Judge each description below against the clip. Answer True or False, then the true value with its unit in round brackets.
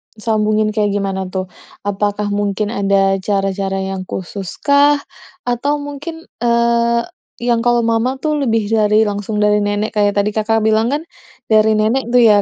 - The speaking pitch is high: True (215 Hz)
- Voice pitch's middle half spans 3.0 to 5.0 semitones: False (2.5 semitones)